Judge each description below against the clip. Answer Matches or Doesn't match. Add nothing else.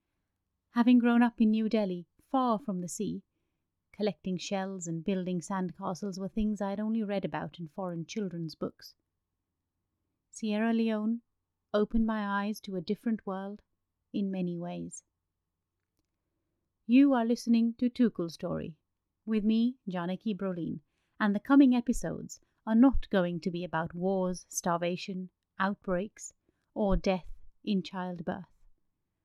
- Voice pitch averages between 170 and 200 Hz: Matches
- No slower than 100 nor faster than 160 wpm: Matches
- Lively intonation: Doesn't match